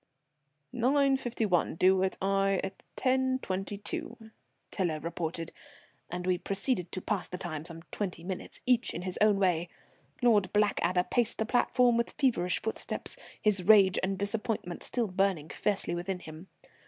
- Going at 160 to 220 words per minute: No, average, 150 wpm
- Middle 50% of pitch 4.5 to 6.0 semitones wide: No, average, 3.7 semitones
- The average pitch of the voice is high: Yes, high, 195 Hz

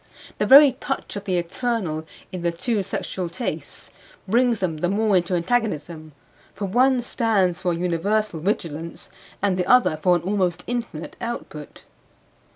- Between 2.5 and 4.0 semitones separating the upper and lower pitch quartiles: No, average, 5.3 semitones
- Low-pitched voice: No, medium, 185 Hz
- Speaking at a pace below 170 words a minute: Yes, average, 155 wpm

